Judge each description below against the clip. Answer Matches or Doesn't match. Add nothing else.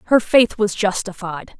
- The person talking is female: Matches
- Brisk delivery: Doesn't match